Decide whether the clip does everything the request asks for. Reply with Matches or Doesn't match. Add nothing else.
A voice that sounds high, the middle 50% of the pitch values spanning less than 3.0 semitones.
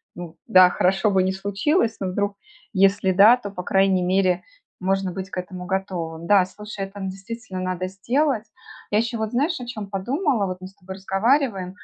Matches